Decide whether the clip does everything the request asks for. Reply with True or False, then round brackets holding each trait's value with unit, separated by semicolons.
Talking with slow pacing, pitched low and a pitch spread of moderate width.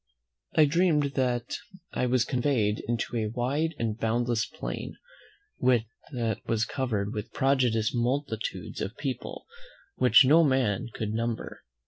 True (125 wpm; 120 Hz; 3.1 semitones)